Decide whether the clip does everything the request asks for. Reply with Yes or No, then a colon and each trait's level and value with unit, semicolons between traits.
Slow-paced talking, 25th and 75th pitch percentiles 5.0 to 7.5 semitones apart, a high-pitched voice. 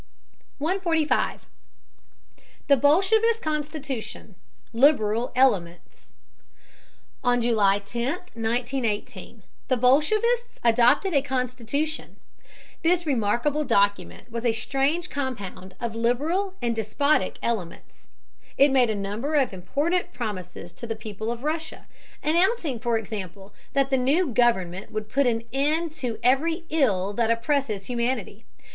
Yes: slow, 115 wpm; average, 5.3 semitones; high, 245 Hz